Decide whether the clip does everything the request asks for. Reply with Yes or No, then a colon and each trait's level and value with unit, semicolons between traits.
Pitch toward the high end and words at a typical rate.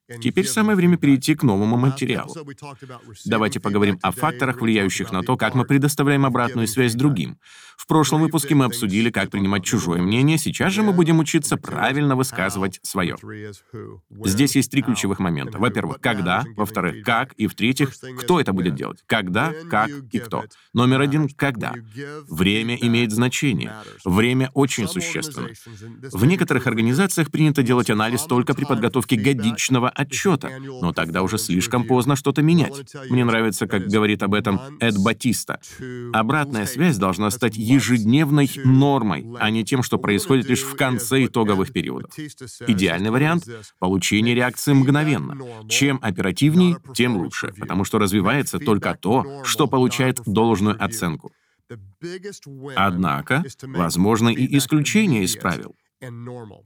No: low, 125 Hz; average, 140 wpm